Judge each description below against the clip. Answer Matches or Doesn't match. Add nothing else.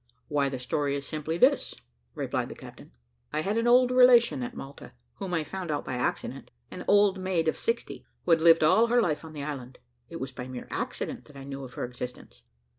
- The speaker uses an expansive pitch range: Matches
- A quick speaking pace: Matches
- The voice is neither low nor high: Matches